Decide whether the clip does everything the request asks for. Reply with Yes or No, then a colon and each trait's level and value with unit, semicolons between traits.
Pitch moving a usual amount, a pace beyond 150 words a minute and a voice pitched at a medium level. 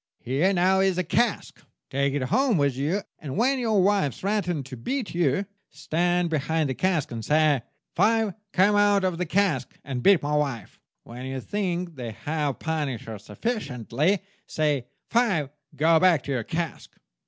No: wide, 6.0 semitones; average, 170 wpm; medium, 160 Hz